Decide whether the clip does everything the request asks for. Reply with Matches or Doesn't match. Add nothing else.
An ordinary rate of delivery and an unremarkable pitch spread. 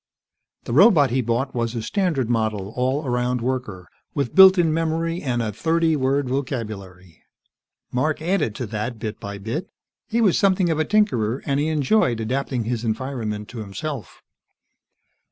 Doesn't match